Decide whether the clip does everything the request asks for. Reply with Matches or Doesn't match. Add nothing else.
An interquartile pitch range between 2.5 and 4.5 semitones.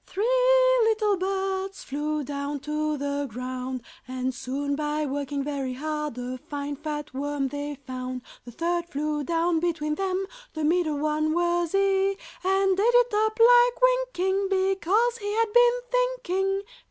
Doesn't match